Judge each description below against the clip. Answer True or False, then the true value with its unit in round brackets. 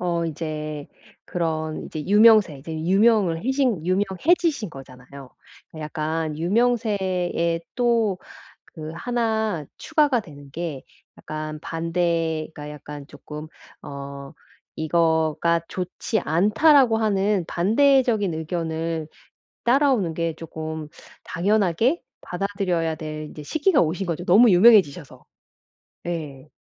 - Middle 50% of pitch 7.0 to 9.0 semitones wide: False (5.4 semitones)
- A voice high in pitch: False (170 Hz)